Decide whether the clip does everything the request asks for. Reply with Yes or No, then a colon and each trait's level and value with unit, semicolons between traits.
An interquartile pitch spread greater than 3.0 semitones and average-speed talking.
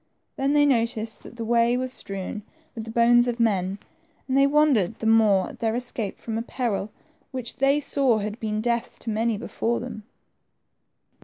No: narrow, 2.4 semitones; average, 180 wpm